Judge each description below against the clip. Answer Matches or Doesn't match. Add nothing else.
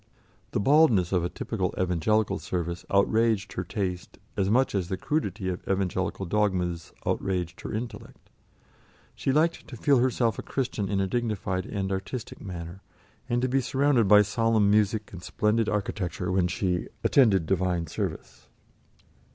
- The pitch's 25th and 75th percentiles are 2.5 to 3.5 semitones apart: Doesn't match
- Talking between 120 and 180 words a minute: Matches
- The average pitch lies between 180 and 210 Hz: Doesn't match